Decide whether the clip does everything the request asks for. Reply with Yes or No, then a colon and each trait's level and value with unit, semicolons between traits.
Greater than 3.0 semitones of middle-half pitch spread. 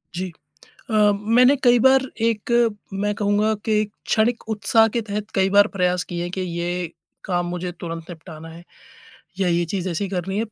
Yes: average, 3.7 semitones